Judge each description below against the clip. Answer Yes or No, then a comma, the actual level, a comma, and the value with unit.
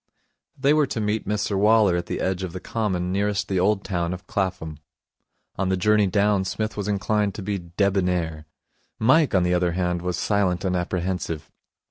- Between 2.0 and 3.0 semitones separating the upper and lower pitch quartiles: Yes, average, 2.7 semitones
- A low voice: Yes, very low, 95 Hz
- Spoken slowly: No, average, 185 wpm